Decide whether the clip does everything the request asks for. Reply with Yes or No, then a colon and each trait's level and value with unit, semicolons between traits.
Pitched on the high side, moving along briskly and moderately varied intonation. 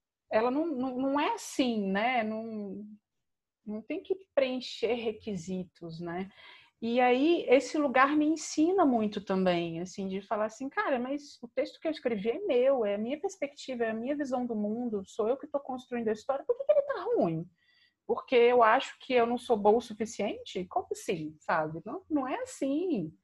No: high, 245 Hz; fast, 195 wpm; wide, 5.7 semitones